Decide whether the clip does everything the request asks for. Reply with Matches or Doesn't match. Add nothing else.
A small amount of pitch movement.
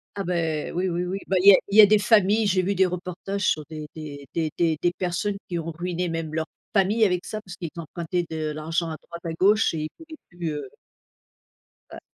Doesn't match